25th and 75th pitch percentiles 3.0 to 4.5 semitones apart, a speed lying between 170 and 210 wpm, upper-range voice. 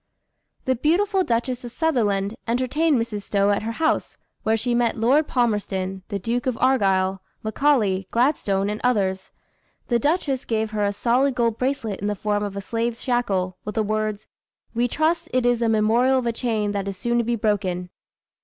Yes: average, 3.6 semitones; average, 185 wpm; high, 230 Hz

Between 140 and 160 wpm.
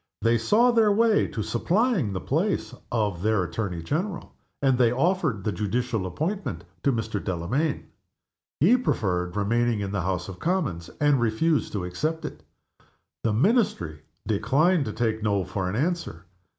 Yes: average, 155 wpm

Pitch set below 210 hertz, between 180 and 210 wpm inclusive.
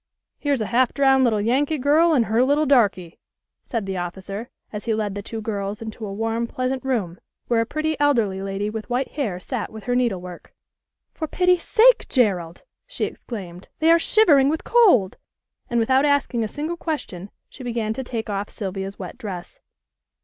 No: high, 230 Hz; average, 185 wpm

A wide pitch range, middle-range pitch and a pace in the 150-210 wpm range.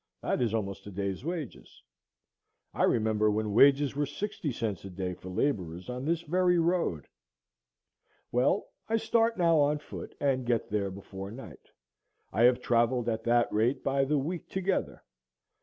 No: wide, 6.2 semitones; low, 125 Hz; average, 160 wpm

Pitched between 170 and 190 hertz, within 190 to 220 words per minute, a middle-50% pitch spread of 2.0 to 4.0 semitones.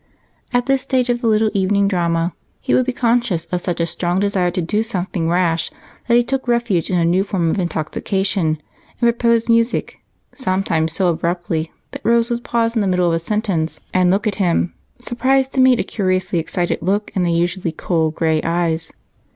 No: medium, 185 Hz; average, 200 wpm; average, 5.3 semitones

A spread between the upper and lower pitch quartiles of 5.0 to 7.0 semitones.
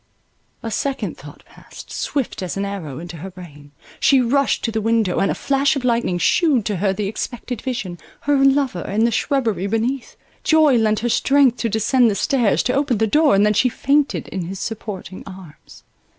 Yes: wide, 5.4 semitones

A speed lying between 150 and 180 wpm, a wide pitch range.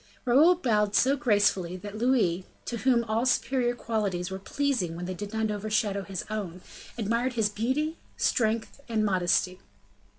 No: average, 155 wpm; average, 3.8 semitones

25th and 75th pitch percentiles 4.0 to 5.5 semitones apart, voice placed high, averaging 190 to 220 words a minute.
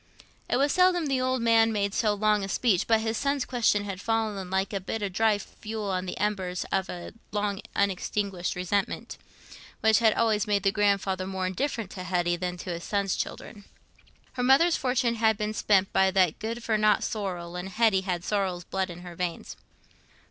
No: average, 3.1 semitones; high, 205 Hz; average, 195 wpm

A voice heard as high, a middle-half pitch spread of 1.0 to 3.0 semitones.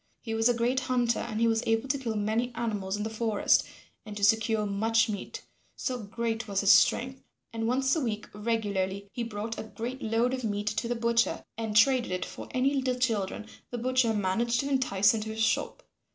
Yes: high, 225 Hz; narrow, 2.4 semitones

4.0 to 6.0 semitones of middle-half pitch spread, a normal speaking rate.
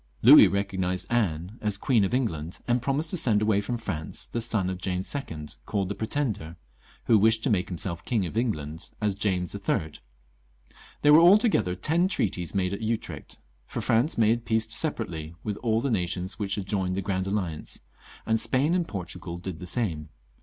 Yes: average, 4.5 semitones; average, 185 wpm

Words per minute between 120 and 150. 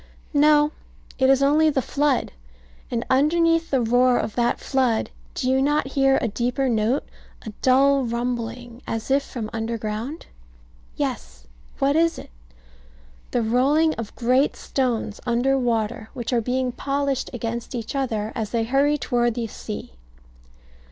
Yes: average, 145 wpm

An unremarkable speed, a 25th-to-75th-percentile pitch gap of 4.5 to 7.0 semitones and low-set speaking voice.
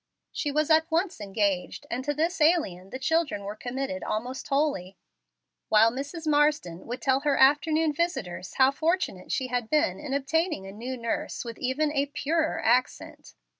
No: average, 170 wpm; average, 5.0 semitones; very high, 275 Hz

